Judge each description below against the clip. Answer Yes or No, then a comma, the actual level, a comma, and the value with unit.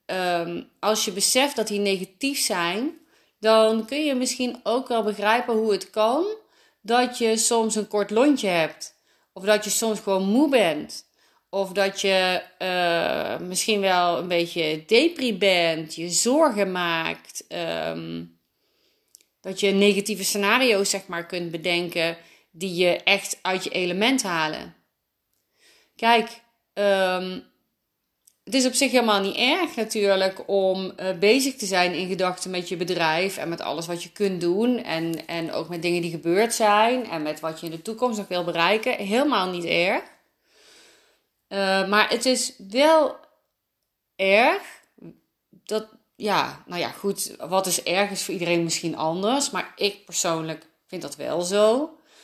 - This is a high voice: Yes, high, 200 Hz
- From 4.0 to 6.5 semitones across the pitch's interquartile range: Yes, average, 4.4 semitones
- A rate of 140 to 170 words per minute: Yes, average, 155 wpm